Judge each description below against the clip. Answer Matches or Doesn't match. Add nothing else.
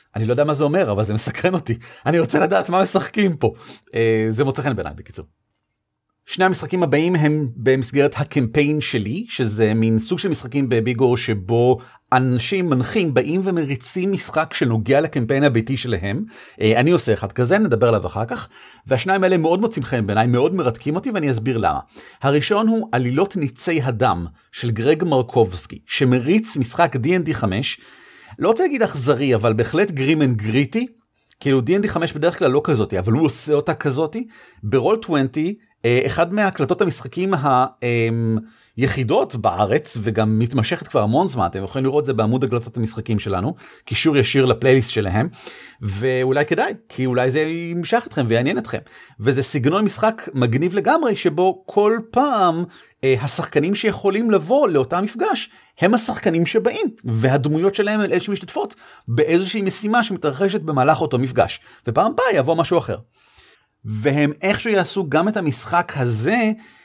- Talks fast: Matches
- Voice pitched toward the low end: Doesn't match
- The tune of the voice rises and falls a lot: Matches